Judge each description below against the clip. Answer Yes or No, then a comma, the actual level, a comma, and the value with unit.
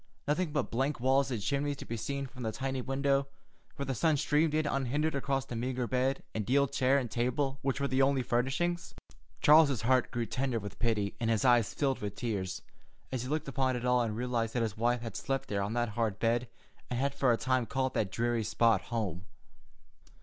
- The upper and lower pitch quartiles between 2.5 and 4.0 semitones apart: Yes, average, 3.0 semitones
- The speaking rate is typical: No, fast, 215 wpm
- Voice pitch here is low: Yes, low, 125 Hz